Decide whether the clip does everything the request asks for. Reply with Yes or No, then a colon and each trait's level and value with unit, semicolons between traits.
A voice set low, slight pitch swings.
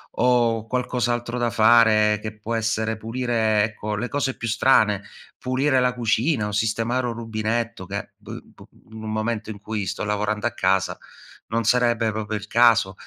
Yes: low, 110 Hz; narrow, 2.0 semitones